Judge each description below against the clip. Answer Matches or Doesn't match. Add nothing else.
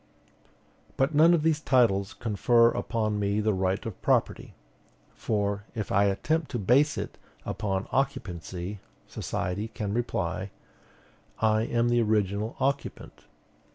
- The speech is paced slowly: Matches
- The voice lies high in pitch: Doesn't match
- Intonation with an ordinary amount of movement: Matches